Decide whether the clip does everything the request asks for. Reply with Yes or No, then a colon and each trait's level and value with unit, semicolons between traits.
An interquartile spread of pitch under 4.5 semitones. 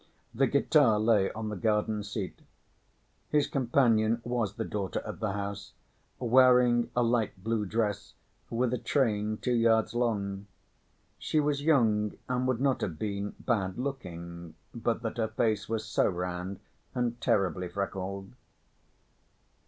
Yes: average, 3.5 semitones